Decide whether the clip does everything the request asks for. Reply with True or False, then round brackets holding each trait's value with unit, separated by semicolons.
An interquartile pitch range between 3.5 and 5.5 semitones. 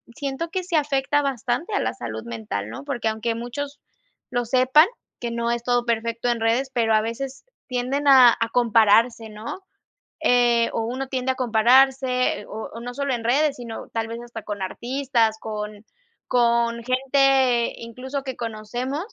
False (2.8 semitones)